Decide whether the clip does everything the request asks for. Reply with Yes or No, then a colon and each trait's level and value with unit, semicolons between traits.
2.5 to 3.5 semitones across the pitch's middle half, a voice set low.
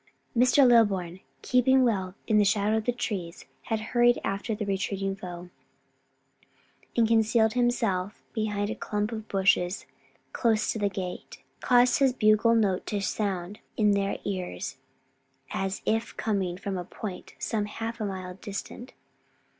No: average, 2.9 semitones; high, 210 Hz